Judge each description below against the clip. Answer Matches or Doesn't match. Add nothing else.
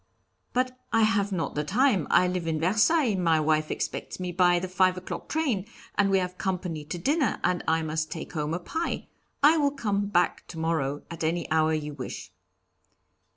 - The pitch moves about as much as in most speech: Matches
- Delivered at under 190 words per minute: Doesn't match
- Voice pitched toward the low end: Doesn't match